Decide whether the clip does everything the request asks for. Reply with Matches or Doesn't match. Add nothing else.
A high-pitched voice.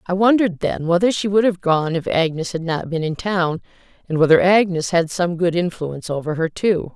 Doesn't match